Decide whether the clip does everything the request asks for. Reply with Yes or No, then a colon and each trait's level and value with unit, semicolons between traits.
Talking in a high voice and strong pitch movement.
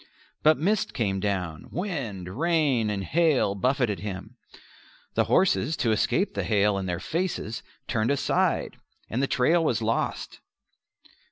No: low, 120 Hz; wide, 7.8 semitones